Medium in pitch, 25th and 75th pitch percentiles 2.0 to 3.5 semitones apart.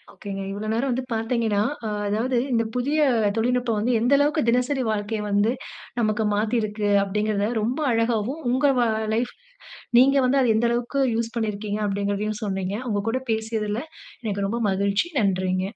No: high, 220 Hz; average, 3.0 semitones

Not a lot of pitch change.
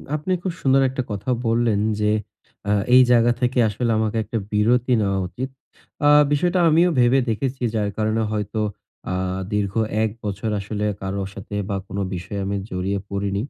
No: average, 3.6 semitones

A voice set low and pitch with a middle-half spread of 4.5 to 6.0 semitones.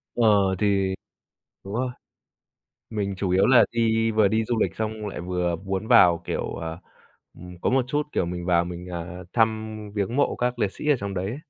No: low, 100 Hz; average, 3.9 semitones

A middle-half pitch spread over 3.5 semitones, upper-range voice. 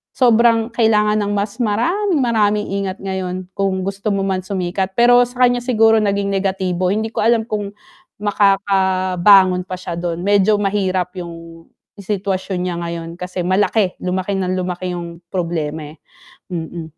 No: narrow, 2.6 semitones; high, 195 Hz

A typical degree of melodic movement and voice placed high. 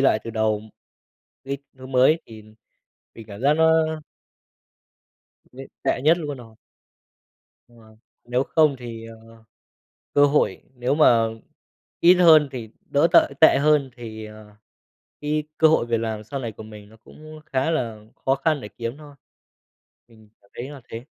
No: average, 4.7 semitones; low, 130 Hz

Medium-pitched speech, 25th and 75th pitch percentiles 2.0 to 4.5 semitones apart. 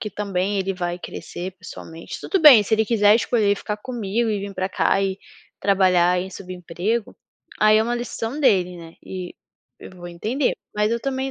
No: high, 200 Hz; average, 3.6 semitones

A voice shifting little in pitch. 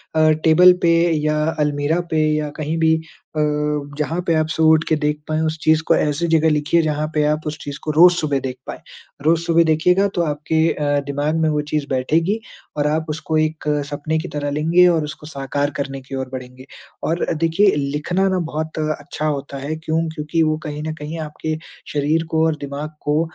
Yes: narrow, 1.6 semitones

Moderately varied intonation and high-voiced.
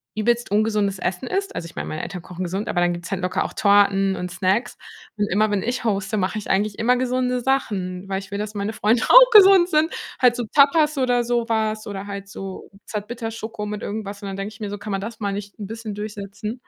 Yes: average, 3.3 semitones; high, 210 Hz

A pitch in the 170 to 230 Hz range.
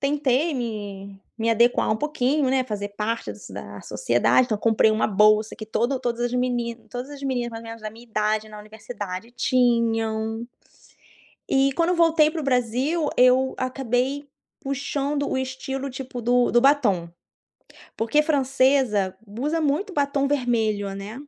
No: high, 245 Hz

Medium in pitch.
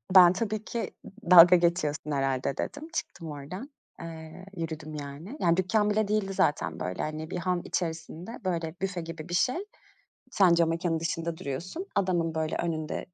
Yes: medium, 170 Hz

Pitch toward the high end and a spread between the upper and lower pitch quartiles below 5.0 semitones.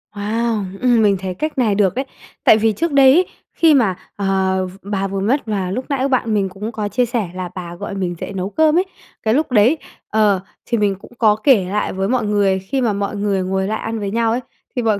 Yes: high, 210 Hz; average, 3.8 semitones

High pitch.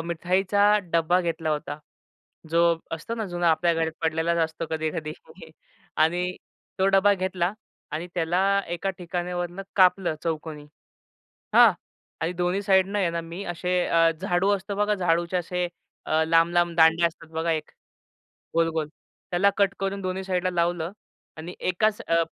No: medium, 175 Hz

